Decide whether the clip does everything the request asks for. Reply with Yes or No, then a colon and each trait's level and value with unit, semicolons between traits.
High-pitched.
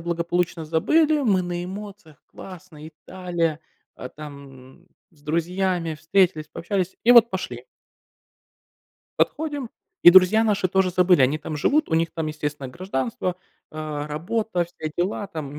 No: medium, 175 Hz